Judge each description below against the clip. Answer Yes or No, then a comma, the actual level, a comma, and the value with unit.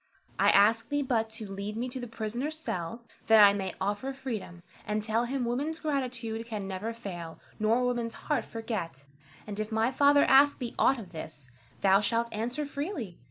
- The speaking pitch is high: Yes, high, 225 Hz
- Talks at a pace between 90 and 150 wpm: No, average, 185 wpm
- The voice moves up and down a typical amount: Yes, average, 3.8 semitones